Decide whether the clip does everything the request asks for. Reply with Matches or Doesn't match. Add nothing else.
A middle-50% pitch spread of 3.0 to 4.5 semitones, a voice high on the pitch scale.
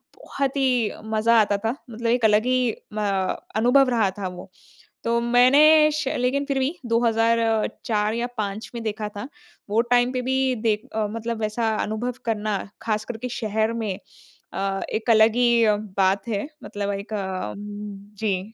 Doesn't match